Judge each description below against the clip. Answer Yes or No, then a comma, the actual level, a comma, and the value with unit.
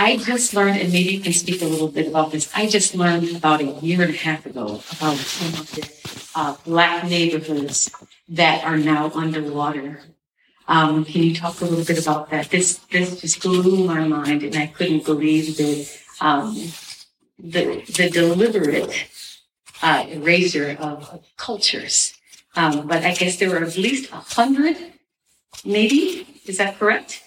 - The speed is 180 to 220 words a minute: No, average, 165 wpm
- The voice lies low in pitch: No, medium, 170 Hz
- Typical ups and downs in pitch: Yes, average, 3.1 semitones